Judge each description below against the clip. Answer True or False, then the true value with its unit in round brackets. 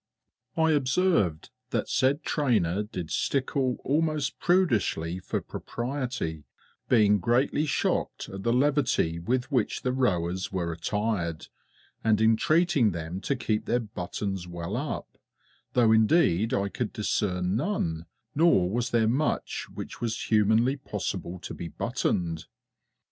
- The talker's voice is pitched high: False (110 Hz)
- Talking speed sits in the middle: False (125 wpm)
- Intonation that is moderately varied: False (6.6 semitones)